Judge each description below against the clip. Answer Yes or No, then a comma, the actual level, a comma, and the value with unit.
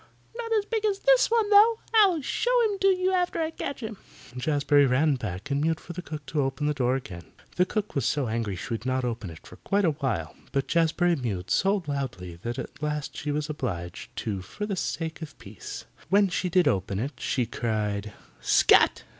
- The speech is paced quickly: Yes, fast, 215 wpm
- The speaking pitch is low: No, medium, 150 Hz